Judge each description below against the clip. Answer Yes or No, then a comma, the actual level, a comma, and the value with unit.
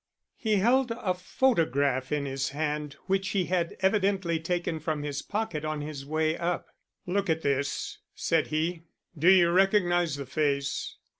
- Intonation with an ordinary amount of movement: Yes, average, 4.3 semitones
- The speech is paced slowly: No, average, 155 wpm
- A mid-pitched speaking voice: Yes, medium, 165 Hz